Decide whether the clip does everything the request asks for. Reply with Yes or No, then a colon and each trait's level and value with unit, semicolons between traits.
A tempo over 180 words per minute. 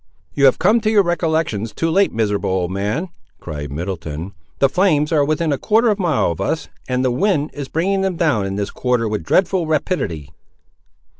Yes: average, 200 wpm